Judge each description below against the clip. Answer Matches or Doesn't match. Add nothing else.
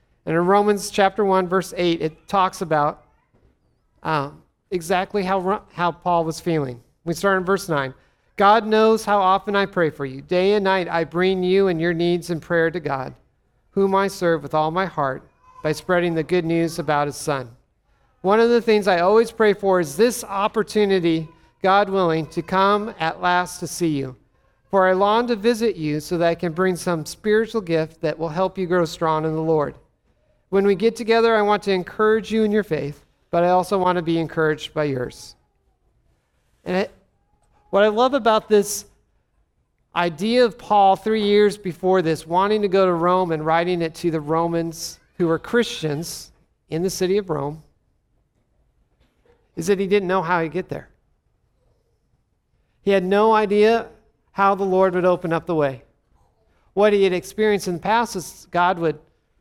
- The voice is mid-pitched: Matches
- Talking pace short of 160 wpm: Doesn't match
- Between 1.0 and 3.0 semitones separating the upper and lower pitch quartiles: Doesn't match